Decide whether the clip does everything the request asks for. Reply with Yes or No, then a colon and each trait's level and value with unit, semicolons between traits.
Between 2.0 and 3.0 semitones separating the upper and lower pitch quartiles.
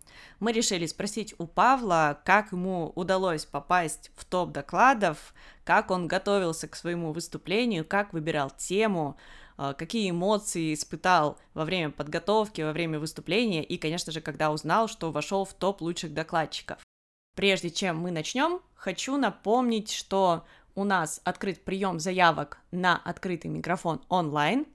No: average, 3.8 semitones